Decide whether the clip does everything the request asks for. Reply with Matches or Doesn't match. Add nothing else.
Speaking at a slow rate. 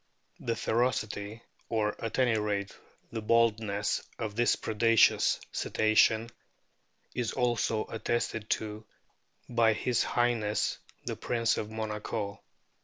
Matches